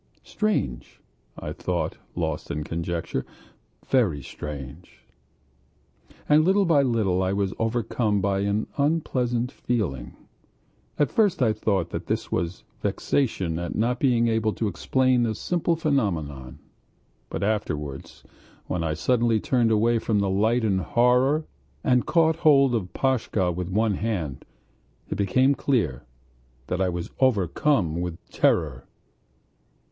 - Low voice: Yes, low, 110 Hz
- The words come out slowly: Yes, slow, 130 wpm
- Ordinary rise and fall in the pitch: No, wide, 6.4 semitones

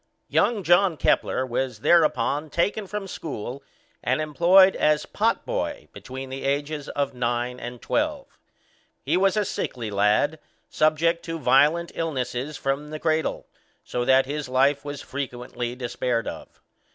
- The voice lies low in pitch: No, medium, 145 Hz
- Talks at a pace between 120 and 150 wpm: Yes, average, 140 wpm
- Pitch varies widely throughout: No, average, 4.6 semitones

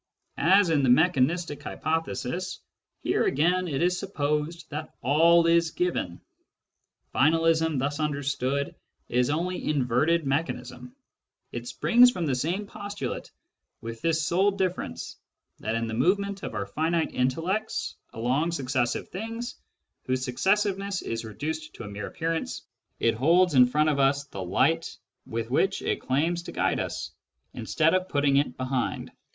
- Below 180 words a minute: Yes, average, 145 wpm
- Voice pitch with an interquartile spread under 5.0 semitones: No, average, 5.3 semitones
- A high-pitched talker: No, medium, 155 Hz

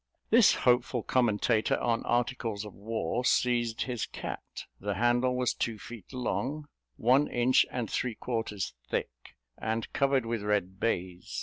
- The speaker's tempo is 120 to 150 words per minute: Yes, average, 140 wpm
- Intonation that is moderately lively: Yes, average, 3.0 semitones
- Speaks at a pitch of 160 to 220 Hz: No, low, 115 Hz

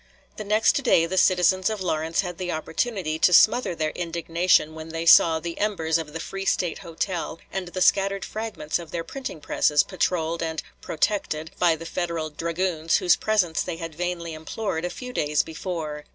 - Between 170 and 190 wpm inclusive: Yes, average, 180 wpm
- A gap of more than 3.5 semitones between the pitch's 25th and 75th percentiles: No, narrow, 2.6 semitones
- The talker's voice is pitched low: No, medium, 170 Hz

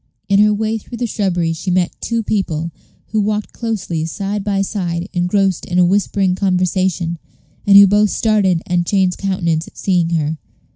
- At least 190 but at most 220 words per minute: No, average, 175 wpm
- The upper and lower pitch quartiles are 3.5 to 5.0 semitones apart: No, average, 2.8 semitones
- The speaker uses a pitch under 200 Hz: Yes, high, 190 Hz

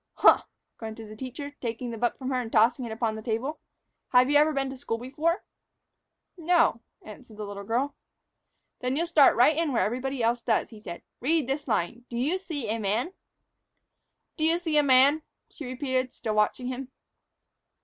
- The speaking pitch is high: Yes, very high, 255 Hz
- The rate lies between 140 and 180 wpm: Yes, average, 175 wpm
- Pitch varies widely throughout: No, average, 4.2 semitones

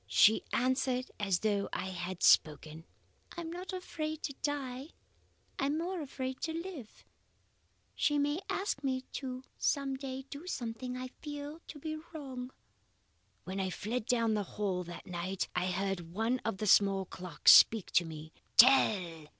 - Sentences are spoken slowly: No, average, 160 wpm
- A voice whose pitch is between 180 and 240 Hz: No, very high, 250 Hz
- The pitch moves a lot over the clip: Yes, wide, 7.2 semitones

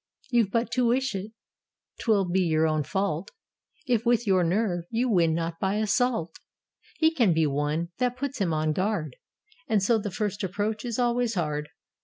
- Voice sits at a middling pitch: No, high, 200 Hz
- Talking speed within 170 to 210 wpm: Yes, average, 190 wpm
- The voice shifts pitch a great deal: Yes, wide, 5.9 semitones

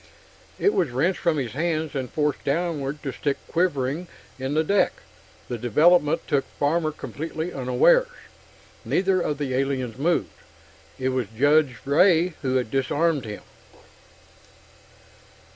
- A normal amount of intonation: Yes, average, 4.1 semitones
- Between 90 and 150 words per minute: Yes, slow, 135 wpm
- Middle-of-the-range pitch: Yes, medium, 145 Hz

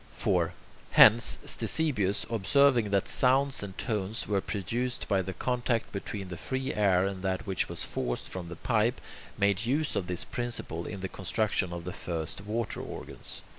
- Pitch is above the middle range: No, low, 100 Hz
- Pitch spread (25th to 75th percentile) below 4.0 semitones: No, average, 4.3 semitones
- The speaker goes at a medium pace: Yes, average, 170 wpm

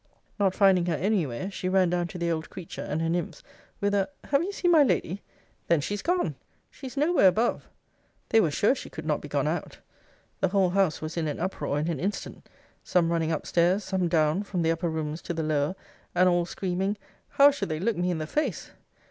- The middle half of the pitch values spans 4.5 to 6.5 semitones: No, average, 3.7 semitones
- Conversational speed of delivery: No, fast, 225 wpm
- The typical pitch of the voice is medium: Yes, medium, 180 Hz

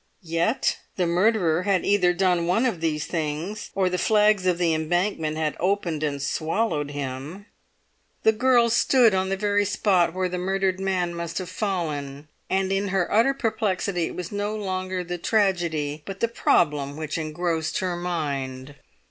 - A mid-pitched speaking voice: Yes, medium, 180 Hz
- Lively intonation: No, average, 3.8 semitones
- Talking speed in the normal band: Yes, average, 165 wpm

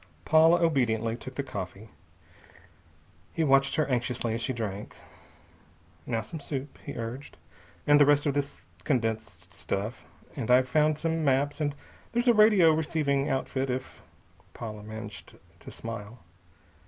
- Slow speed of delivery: No, average, 145 wpm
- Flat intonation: No, average, 4.7 semitones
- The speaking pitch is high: No, low, 130 Hz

